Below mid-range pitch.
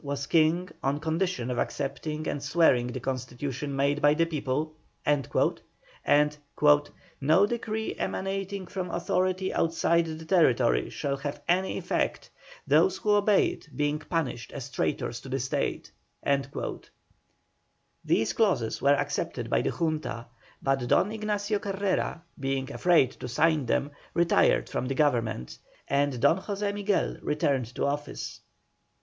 No: medium, 150 Hz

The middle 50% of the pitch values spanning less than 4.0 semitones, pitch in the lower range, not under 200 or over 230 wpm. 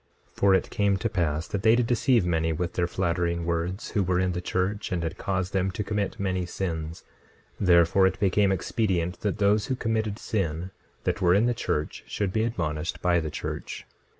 Yes: average, 3.0 semitones; very low, 95 Hz; fast, 205 wpm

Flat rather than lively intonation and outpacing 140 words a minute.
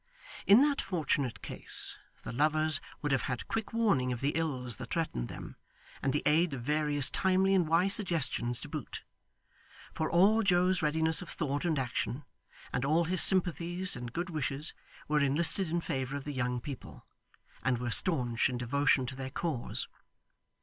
No: average, 4.9 semitones; average, 170 wpm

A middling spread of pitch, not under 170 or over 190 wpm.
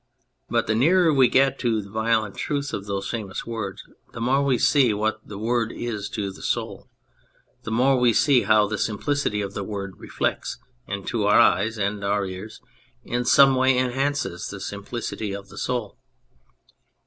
Yes: average, 3.9 semitones; average, 180 wpm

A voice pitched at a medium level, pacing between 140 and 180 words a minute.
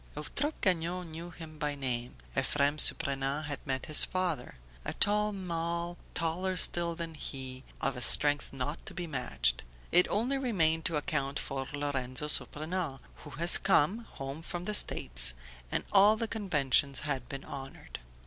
Yes: medium, 155 Hz; average, 160 wpm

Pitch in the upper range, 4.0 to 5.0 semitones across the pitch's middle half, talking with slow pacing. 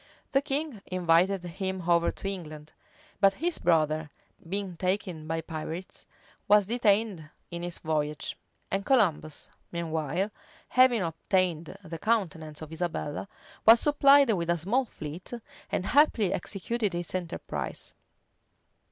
No: medium, 180 Hz; average, 4.3 semitones; slow, 125 wpm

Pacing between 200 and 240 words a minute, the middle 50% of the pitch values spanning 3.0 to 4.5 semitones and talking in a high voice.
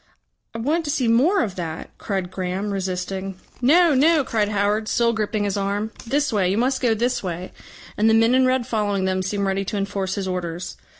Yes: fast, 205 wpm; average, 4.2 semitones; high, 210 Hz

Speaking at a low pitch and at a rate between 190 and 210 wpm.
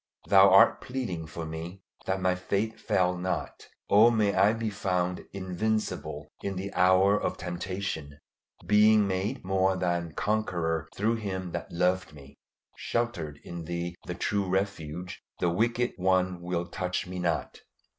No: very low, 95 Hz; average, 145 wpm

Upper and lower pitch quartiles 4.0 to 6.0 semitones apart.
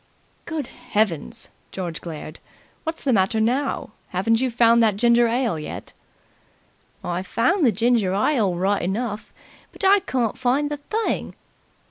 Yes: average, 5.2 semitones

